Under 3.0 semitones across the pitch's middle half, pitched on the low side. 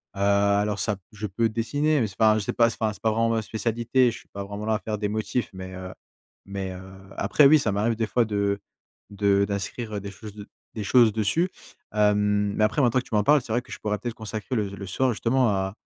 Yes: narrow, 2.4 semitones; low, 105 Hz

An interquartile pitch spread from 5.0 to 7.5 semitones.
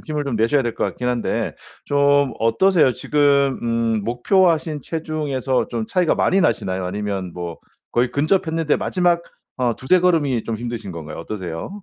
Yes: wide, 5.6 semitones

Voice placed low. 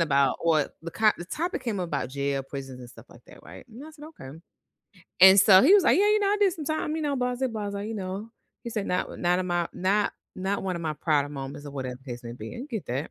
No: medium, 185 Hz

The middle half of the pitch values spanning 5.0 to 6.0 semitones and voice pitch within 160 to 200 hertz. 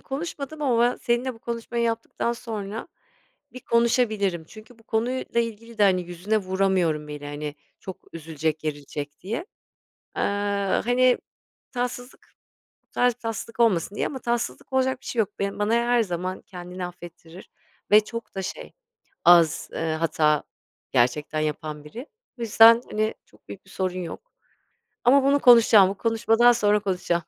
No: average, 5.3 semitones; high, 210 Hz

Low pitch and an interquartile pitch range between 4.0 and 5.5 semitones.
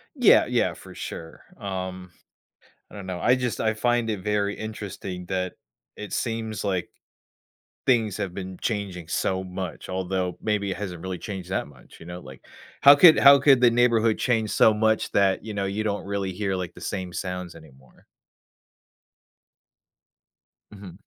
No: low, 100 Hz; average, 3.1 semitones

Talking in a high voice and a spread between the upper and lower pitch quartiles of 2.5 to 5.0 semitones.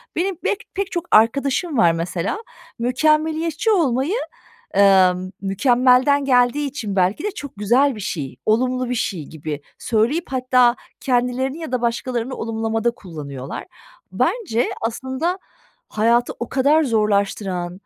No: high, 245 Hz; wide, 5.6 semitones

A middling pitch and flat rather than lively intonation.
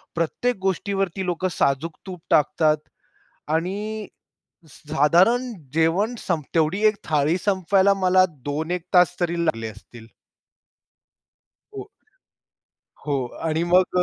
No: medium, 175 Hz; average, 3.7 semitones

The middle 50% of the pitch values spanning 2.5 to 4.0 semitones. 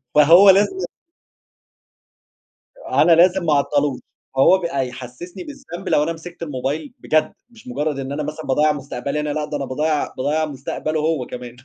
Yes: average, 3.3 semitones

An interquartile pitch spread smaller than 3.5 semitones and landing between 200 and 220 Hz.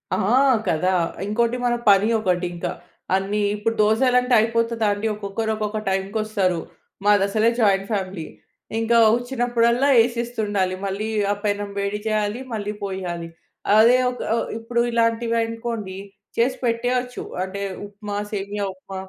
Yes: average, 2.8 semitones; high, 215 Hz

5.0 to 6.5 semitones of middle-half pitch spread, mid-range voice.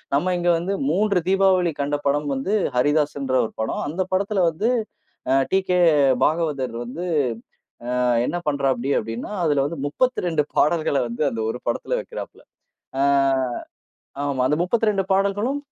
Yes: wide, 5.6 semitones; medium, 160 Hz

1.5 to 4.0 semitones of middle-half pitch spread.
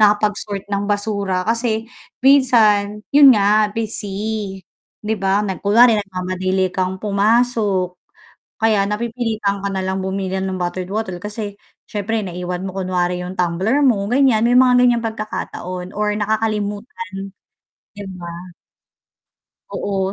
Yes: narrow, 2.6 semitones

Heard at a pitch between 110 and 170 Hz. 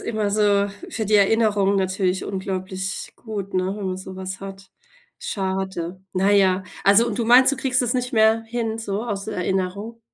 No: high, 200 Hz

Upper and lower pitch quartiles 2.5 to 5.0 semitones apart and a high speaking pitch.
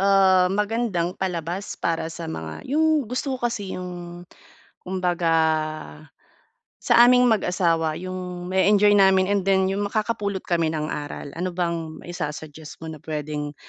No: average, 3.3 semitones; medium, 180 Hz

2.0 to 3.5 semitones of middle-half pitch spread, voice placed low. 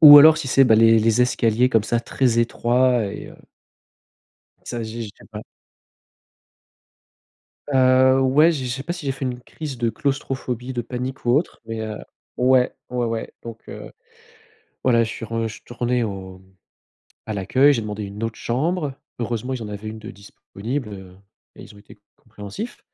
Yes: average, 2.9 semitones; low, 120 Hz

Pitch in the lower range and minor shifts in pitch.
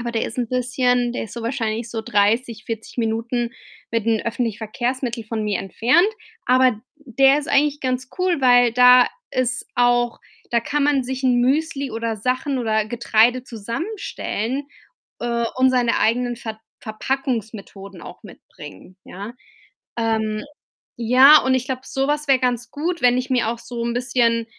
No: high, 240 Hz; narrow, 2.3 semitones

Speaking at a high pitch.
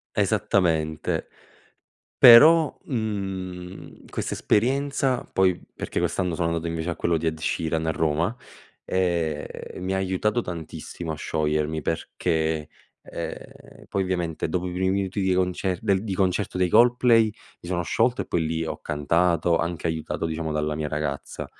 No: very low, 90 Hz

